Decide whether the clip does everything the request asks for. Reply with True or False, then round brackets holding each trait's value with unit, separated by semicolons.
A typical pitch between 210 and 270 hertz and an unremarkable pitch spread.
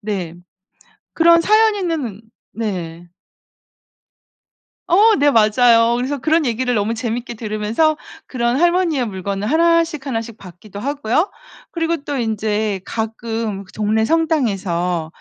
False (230 Hz; 6.8 semitones)